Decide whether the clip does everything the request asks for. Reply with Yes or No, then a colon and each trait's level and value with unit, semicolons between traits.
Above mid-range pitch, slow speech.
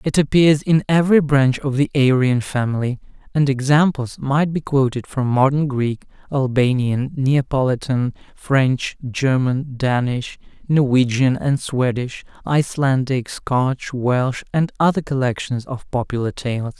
No: low, 135 Hz; slow, 120 wpm